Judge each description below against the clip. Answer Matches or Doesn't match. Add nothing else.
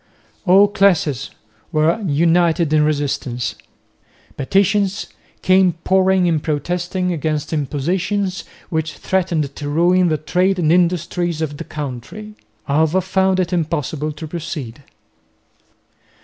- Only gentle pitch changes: Doesn't match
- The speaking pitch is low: Doesn't match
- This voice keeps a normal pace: Doesn't match